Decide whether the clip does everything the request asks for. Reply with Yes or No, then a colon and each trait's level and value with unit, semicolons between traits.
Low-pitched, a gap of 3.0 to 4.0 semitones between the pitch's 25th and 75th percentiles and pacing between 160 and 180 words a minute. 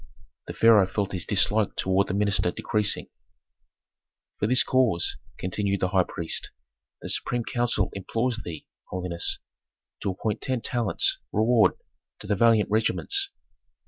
No: low, 105 Hz; average, 3.5 semitones; slow, 135 wpm